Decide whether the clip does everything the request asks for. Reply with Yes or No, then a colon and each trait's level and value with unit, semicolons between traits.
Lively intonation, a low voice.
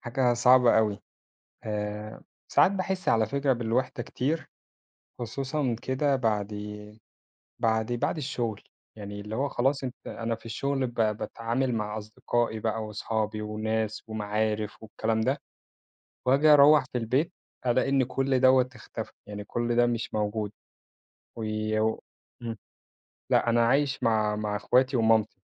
No: average, 3.3 semitones; low, 115 Hz